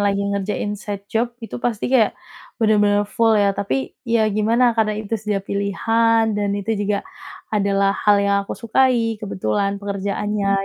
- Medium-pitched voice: No, high, 205 Hz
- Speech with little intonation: Yes, narrow, 2.0 semitones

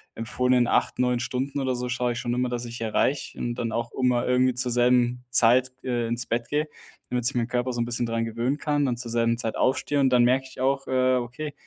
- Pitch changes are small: Yes, narrow, 1.4 semitones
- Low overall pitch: Yes, low, 125 Hz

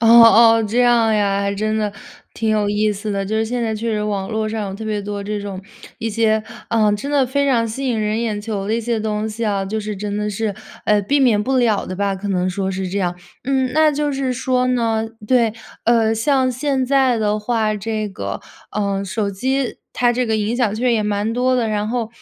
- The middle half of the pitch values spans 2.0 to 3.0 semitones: Yes, narrow, 2.6 semitones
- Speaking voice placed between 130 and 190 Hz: No, high, 220 Hz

